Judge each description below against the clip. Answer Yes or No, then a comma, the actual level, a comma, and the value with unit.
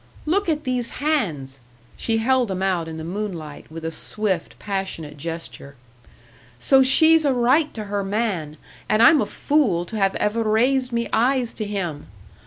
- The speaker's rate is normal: Yes, average, 170 wpm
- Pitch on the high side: Yes, high, 215 Hz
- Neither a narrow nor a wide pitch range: No, wide, 7.2 semitones